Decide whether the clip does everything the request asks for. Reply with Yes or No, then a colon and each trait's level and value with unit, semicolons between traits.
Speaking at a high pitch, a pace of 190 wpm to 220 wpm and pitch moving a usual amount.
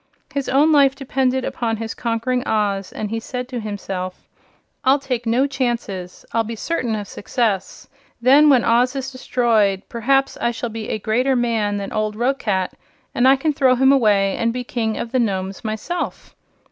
No: high, 235 Hz; average, 180 wpm; average, 3.5 semitones